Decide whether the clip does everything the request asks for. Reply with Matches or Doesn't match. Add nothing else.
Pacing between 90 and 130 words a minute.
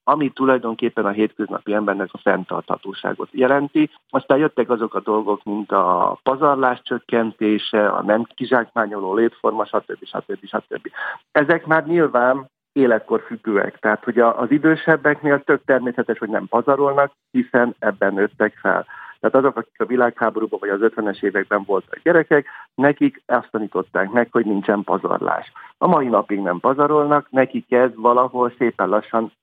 Doesn't match